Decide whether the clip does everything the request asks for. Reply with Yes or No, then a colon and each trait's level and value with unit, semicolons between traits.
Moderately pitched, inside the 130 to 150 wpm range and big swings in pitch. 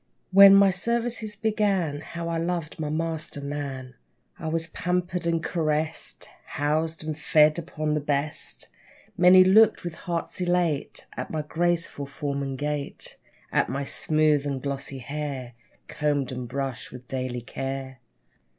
No: medium, 155 Hz; average, 140 wpm; average, 3.7 semitones